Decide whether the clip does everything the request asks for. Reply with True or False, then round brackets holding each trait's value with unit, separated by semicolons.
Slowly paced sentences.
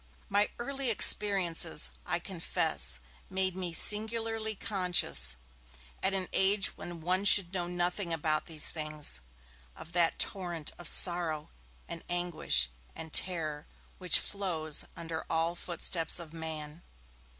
True (125 wpm)